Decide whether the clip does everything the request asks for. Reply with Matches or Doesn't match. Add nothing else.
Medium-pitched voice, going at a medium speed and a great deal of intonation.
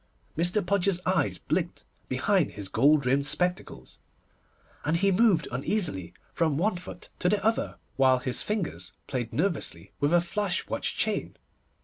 Matches